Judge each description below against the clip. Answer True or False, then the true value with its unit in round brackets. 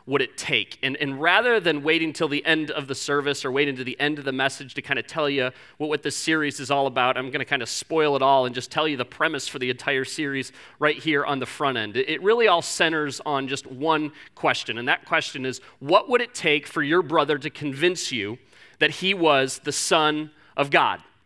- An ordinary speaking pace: False (245 wpm)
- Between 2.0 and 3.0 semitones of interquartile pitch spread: True (2.6 semitones)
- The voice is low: False (145 Hz)